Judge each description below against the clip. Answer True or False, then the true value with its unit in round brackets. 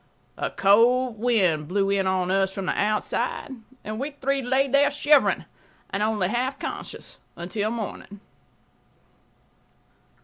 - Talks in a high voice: True (215 Hz)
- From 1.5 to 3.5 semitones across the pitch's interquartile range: False (4.8 semitones)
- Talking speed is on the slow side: True (130 wpm)